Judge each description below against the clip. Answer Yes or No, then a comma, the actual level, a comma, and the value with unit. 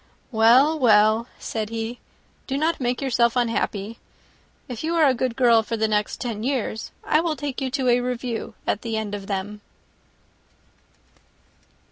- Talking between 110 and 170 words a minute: Yes, average, 160 wpm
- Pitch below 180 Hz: No, high, 235 Hz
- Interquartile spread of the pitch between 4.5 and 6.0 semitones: No, average, 3.0 semitones